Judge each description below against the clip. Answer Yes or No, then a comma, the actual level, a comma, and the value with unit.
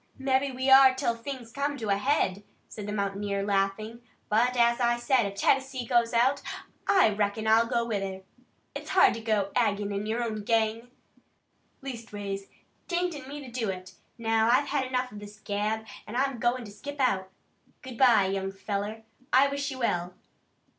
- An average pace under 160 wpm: No, average, 185 wpm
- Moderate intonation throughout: Yes, average, 4.1 semitones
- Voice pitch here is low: No, high, 230 Hz